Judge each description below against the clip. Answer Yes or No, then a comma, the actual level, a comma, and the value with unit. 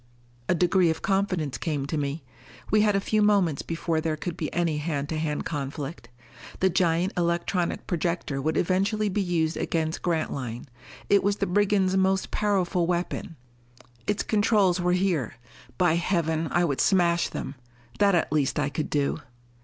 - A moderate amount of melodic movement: Yes, average, 3.4 semitones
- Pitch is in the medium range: Yes, medium, 170 Hz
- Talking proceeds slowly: No, average, 165 wpm